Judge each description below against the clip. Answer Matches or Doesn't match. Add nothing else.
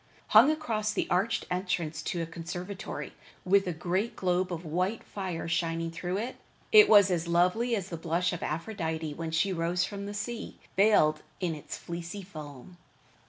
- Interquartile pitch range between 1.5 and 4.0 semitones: Matches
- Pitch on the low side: Doesn't match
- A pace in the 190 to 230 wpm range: Doesn't match